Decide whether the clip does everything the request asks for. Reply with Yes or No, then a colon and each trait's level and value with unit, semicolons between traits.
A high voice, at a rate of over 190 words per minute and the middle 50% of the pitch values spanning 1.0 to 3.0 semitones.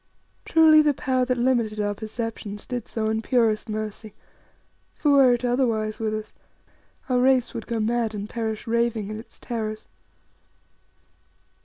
No: high, 230 Hz; average, 150 wpm; narrow, 2.5 semitones